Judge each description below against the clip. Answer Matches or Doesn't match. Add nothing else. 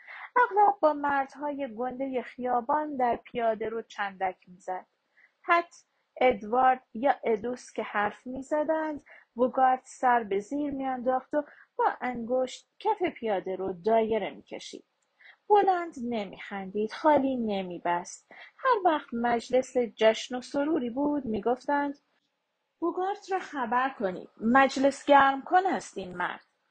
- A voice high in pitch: Matches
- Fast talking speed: Doesn't match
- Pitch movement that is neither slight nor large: Matches